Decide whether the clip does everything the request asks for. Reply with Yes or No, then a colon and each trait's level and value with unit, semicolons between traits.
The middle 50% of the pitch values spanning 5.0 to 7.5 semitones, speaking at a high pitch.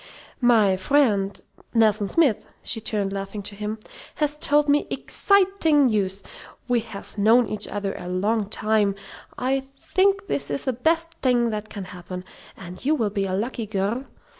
Yes: average, 5.3 semitones; high, 215 Hz